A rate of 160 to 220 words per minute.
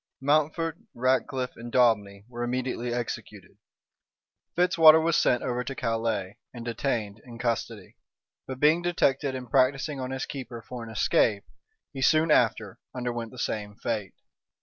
No: average, 145 wpm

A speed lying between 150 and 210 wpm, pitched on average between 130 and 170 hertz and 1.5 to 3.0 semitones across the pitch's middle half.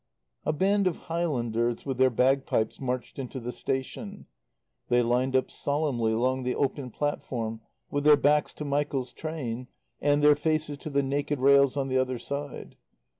Yes: average, 165 wpm; low, 135 Hz; average, 2.7 semitones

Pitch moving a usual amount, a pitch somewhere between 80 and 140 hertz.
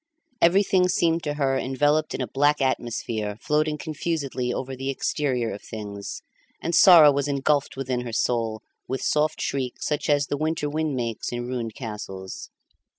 Yes: average, 3.9 semitones; low, 135 Hz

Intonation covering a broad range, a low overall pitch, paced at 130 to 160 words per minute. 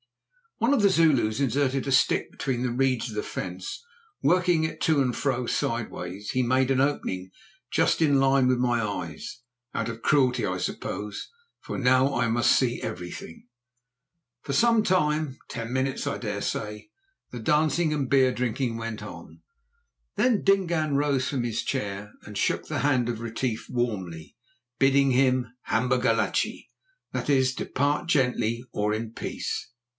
No: average, 3.6 semitones; low, 130 Hz; average, 155 wpm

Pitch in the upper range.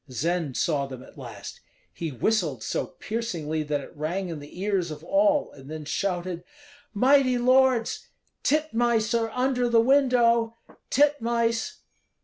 Yes: high, 225 Hz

